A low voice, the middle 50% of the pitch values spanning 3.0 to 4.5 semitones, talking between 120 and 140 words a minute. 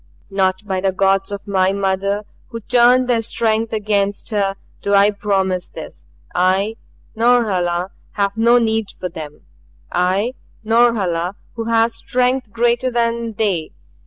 No: high, 205 Hz; average, 3.3 semitones; slow, 135 wpm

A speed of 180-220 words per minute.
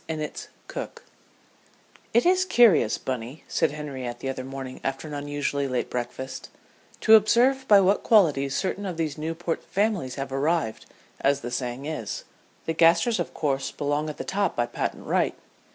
No: average, 165 wpm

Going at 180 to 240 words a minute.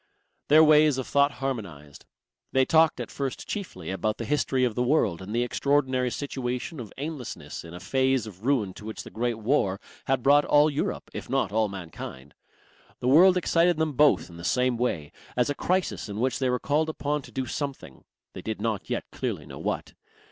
Yes: average, 200 wpm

